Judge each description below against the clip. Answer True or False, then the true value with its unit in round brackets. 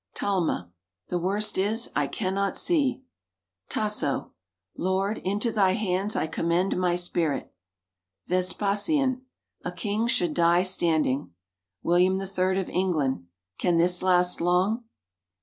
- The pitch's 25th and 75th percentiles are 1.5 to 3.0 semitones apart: True (2.7 semitones)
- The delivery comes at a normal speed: False (115 wpm)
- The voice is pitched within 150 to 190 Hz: True (185 Hz)